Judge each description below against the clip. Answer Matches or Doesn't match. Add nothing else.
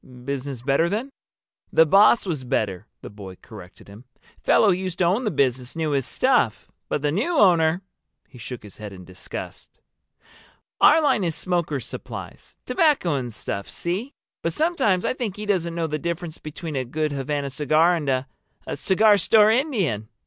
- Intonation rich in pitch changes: Matches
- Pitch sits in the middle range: Matches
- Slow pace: Doesn't match